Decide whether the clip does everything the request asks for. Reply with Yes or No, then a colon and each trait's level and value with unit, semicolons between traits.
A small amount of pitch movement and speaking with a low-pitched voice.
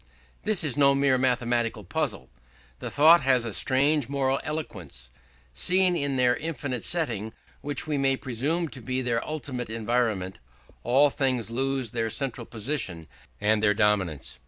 No: average, 4.3 semitones; low, 130 Hz